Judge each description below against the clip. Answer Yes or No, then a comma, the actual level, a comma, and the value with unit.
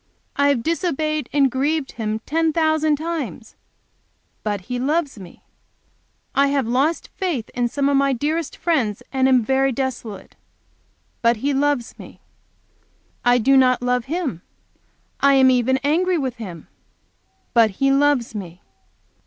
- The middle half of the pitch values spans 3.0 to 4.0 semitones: Yes, average, 3.7 semitones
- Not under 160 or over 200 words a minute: No, average, 145 wpm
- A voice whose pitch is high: Yes, very high, 270 Hz